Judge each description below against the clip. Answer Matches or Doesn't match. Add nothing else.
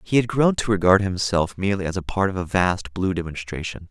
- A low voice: Matches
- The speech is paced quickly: Matches